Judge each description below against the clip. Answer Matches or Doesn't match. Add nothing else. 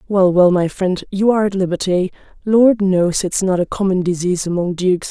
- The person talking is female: Matches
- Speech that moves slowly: Doesn't match